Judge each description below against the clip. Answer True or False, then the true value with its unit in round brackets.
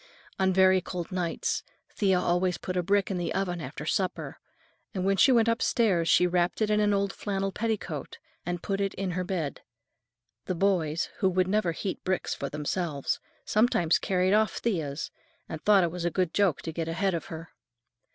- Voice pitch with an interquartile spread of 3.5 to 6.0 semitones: False (2.6 semitones)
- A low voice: False (185 Hz)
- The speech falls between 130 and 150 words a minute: False (190 wpm)